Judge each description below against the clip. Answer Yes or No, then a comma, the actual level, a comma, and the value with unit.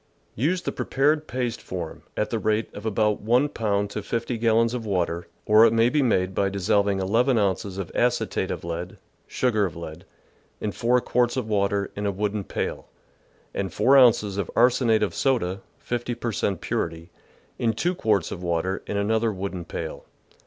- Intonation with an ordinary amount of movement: Yes, average, 3.7 semitones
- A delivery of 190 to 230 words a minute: Yes, average, 195 wpm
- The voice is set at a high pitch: No, low, 105 Hz